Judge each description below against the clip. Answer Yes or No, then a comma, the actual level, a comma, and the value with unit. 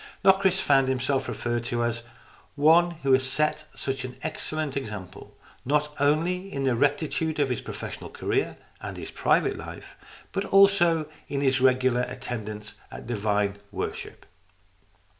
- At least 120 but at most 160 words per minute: Yes, average, 145 wpm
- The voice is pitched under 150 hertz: Yes, low, 135 Hz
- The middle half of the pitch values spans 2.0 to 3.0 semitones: No, average, 4.1 semitones